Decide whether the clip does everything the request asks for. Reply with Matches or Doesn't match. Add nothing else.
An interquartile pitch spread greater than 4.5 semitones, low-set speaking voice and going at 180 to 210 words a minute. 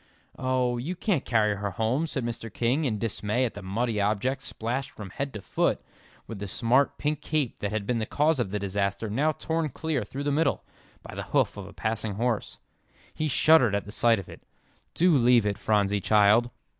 Matches